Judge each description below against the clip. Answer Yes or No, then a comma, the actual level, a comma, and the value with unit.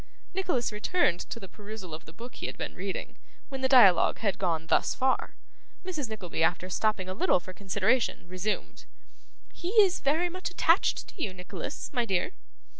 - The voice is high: Yes, high, 215 Hz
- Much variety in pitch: Yes, wide, 6.3 semitones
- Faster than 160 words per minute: Yes, average, 180 wpm